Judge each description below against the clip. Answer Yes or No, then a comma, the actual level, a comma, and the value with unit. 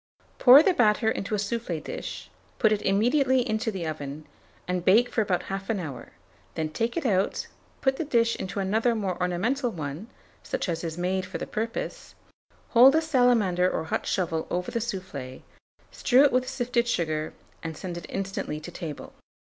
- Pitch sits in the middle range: No, high, 195 Hz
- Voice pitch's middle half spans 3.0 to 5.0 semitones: No, wide, 5.5 semitones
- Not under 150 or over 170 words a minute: No, average, 180 wpm